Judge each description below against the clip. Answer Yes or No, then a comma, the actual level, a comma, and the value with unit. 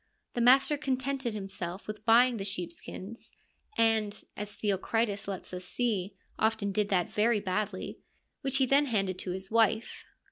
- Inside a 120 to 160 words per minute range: No, average, 170 wpm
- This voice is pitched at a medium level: No, high, 215 Hz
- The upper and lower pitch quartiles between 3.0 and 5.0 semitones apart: Yes, average, 3.5 semitones